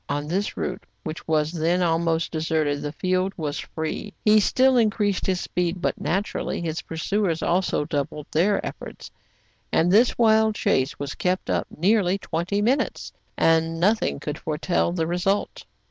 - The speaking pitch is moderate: Yes, medium, 175 Hz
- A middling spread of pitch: Yes, average, 4.0 semitones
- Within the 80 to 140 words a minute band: No, average, 155 wpm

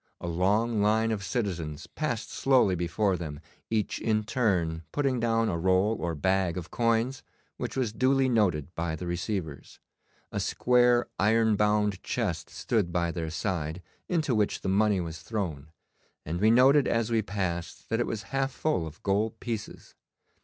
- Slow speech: No, average, 165 wpm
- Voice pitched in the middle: No, low, 105 Hz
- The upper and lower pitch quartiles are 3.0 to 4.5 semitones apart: No, average, 4.9 semitones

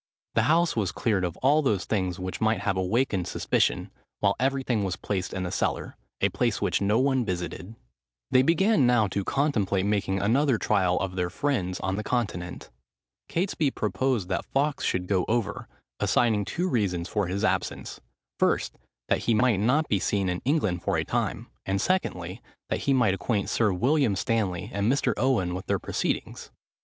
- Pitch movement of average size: No, wide, 5.7 semitones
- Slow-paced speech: No, average, 175 wpm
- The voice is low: Yes, low, 105 Hz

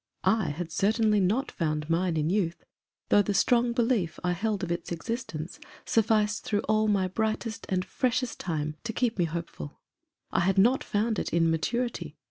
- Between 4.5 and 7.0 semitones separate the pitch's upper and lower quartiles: Yes, average, 4.9 semitones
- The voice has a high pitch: Yes, high, 200 Hz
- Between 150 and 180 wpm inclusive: Yes, average, 175 wpm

